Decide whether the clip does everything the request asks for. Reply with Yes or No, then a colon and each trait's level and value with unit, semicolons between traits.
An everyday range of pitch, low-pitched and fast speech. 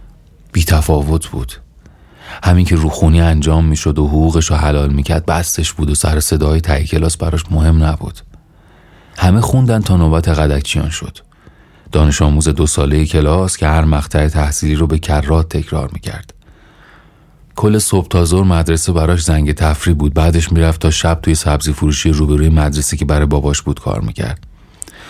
No: narrow, 1.8 semitones; very low, 80 Hz; fast, 165 wpm